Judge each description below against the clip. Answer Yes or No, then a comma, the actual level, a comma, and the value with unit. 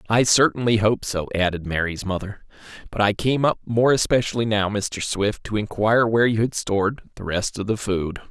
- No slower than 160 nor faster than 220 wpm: Yes, average, 195 wpm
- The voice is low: Yes, low, 105 Hz